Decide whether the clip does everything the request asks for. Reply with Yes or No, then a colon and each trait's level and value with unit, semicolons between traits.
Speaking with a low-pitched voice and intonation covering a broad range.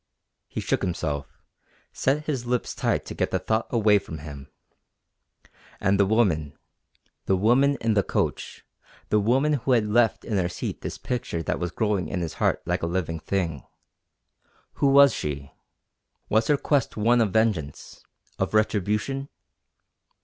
Yes: low, 105 Hz; wide, 5.7 semitones